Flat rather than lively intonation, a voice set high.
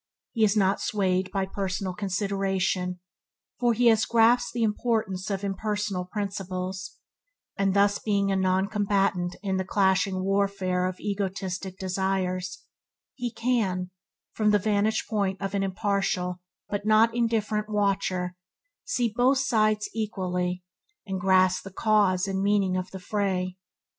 Yes: narrow, 2.2 semitones; high, 195 Hz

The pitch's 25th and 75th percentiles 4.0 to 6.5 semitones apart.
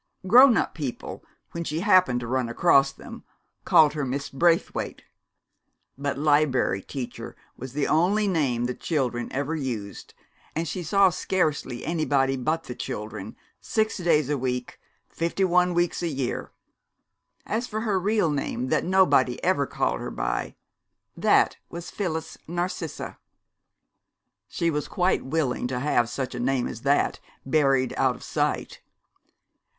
Yes: average, 5.1 semitones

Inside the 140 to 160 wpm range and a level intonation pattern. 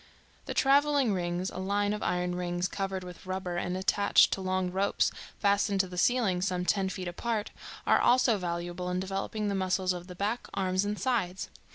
No: average, 190 wpm; narrow, 2.2 semitones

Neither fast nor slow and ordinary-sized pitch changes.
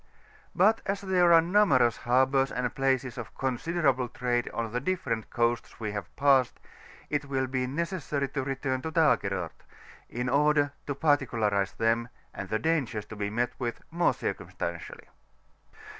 Yes: average, 155 wpm; average, 4.0 semitones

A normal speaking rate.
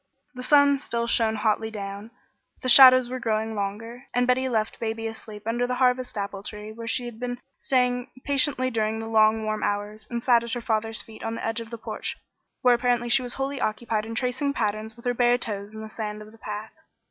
No: fast, 225 wpm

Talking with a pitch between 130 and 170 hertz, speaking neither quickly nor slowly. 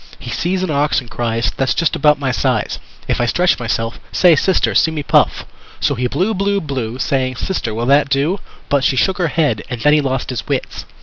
No: medium, 140 Hz; fast, 225 wpm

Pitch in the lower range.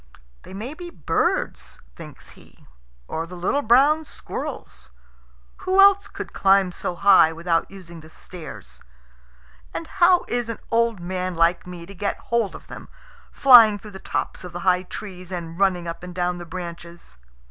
No: medium, 185 Hz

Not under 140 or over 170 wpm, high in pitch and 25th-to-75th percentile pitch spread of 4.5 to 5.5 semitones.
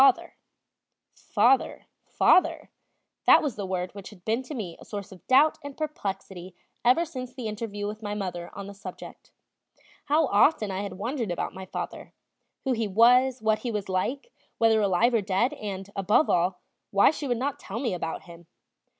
No: average, 180 wpm; high, 215 Hz; average, 5.1 semitones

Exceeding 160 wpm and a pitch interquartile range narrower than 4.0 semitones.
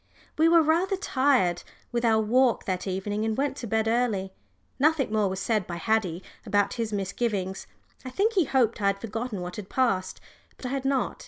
No: average, 195 wpm; average, 5.0 semitones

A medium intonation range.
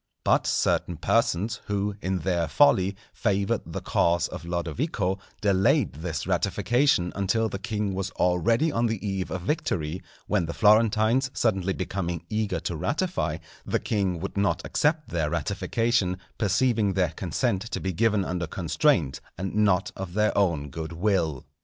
Yes: average, 3.8 semitones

